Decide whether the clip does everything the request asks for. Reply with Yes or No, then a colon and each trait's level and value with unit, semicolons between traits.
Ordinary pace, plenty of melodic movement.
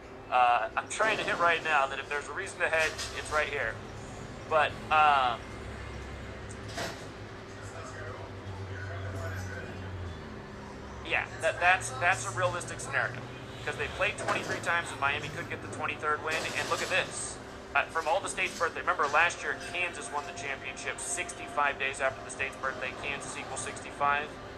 Yes: average, 155 wpm; wide, 6.8 semitones